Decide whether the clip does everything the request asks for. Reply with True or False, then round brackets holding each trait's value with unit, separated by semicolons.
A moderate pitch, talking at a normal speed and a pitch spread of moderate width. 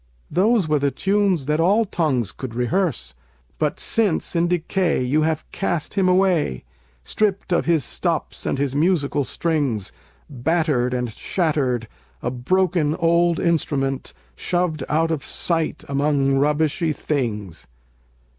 False (155 Hz; 130 wpm; 4.4 semitones)